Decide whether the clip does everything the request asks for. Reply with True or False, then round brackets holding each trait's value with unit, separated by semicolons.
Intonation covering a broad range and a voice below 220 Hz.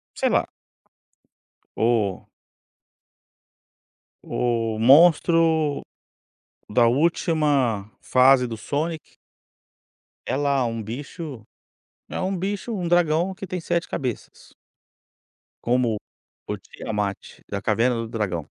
True (6.4 semitones; 135 Hz)